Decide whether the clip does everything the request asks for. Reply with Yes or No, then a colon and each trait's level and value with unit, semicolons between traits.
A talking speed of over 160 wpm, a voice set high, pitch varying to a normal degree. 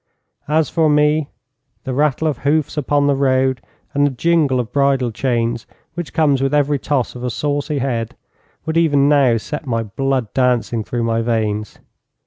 No: average, 170 wpm; low, 135 Hz; average, 3.4 semitones